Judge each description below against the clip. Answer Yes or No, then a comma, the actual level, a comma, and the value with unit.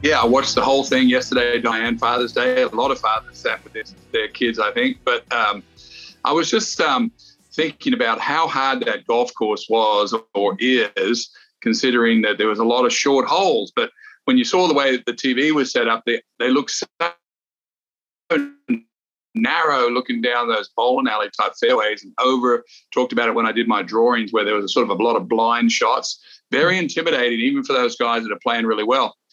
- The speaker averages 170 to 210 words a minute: Yes, fast, 205 wpm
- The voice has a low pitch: Yes, low, 130 Hz